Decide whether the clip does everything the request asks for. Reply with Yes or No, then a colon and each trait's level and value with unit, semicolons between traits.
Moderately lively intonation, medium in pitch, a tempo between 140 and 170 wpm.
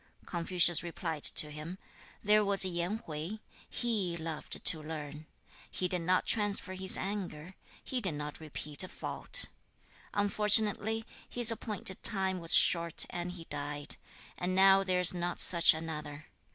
Yes: average, 3.7 semitones; medium, 180 Hz; average, 145 wpm